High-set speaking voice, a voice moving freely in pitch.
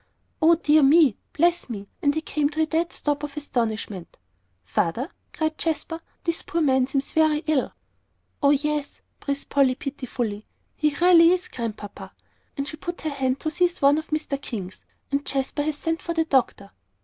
No: very high, 290 Hz; average, 3.2 semitones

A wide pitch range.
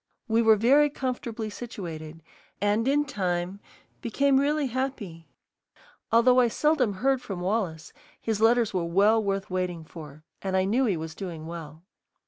Yes: wide, 6.0 semitones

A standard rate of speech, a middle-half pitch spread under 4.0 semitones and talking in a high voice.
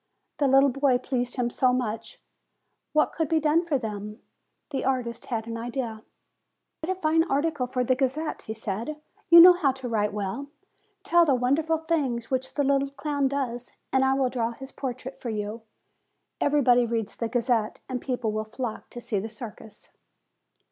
Yes: average, 180 wpm; average, 3.5 semitones; very high, 255 Hz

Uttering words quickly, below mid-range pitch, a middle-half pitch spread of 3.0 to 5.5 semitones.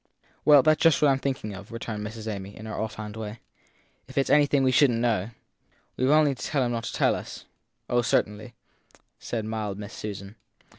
Yes: fast, 225 wpm; low, 115 Hz; average, 4.2 semitones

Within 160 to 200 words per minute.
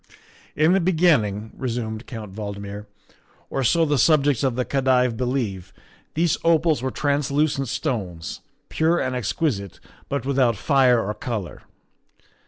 No: average, 140 wpm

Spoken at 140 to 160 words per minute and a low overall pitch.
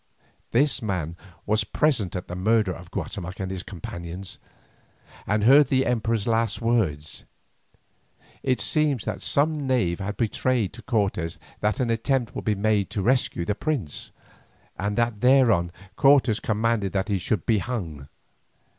Yes: average, 150 wpm; low, 110 Hz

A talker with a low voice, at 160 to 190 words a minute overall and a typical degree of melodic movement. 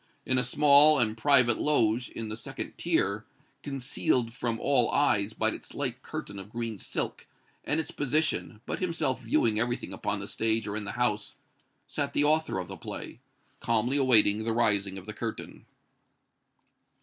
Yes: low, 115 Hz; average, 170 wpm; average, 4.1 semitones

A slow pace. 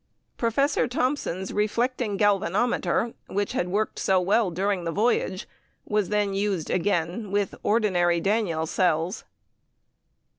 Yes: slow, 115 wpm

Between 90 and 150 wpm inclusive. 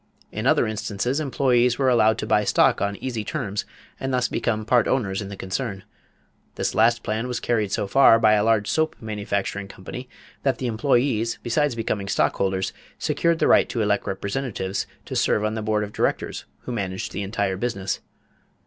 No: average, 185 wpm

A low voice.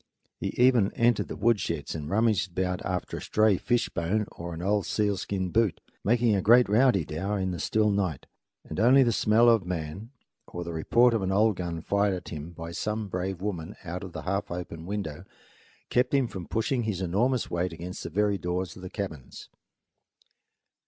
Yes: very low, 95 Hz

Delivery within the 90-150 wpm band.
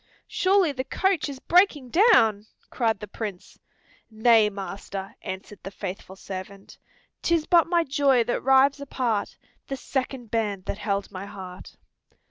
Yes: average, 140 wpm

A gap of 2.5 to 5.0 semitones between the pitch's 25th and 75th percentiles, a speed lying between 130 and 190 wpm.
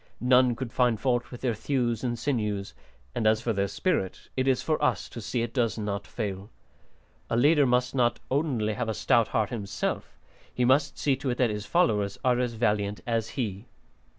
No: average, 3.0 semitones; average, 200 wpm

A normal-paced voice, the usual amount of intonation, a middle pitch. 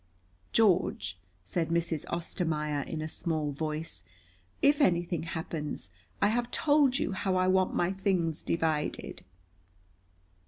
No: slow, 120 wpm; average, 3.4 semitones; medium, 170 Hz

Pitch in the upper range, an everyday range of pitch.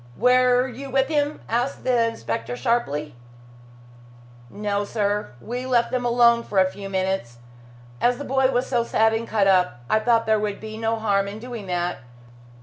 Yes: high, 225 Hz; average, 3.8 semitones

